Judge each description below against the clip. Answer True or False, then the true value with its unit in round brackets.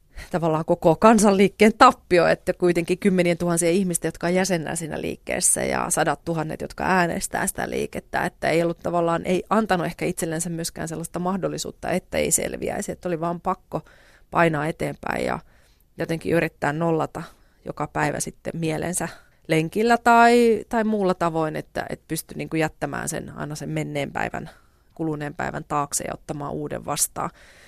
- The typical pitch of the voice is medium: True (170 Hz)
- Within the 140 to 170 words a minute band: True (150 wpm)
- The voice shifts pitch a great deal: False (2.5 semitones)